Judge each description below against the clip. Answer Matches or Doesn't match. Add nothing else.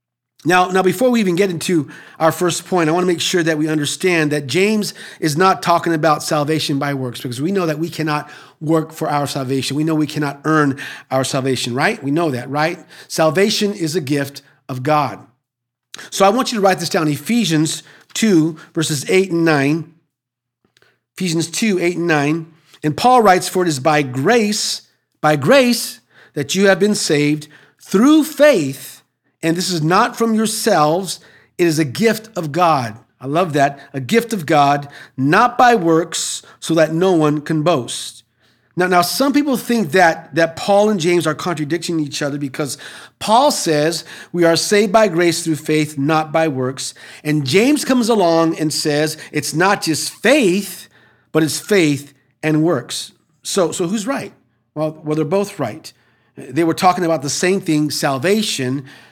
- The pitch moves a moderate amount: Matches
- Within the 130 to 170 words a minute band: Doesn't match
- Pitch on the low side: Doesn't match